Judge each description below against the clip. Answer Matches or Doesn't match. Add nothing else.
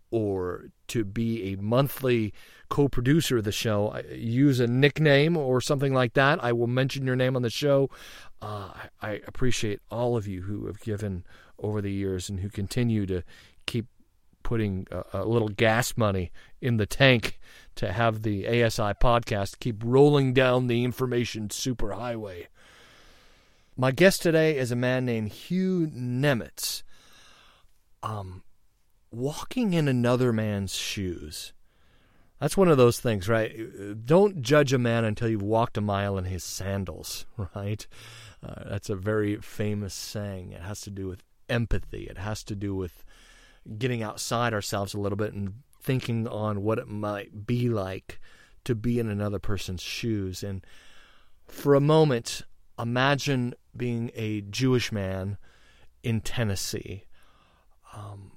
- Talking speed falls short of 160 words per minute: Matches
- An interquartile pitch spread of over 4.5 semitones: Doesn't match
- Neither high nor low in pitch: Doesn't match